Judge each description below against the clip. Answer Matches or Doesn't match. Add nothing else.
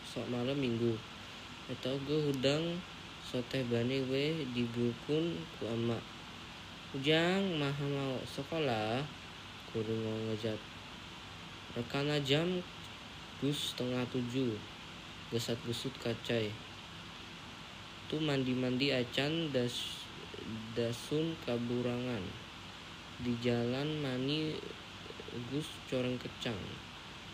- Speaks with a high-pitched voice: Doesn't match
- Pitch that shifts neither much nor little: Matches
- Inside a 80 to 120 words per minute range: Matches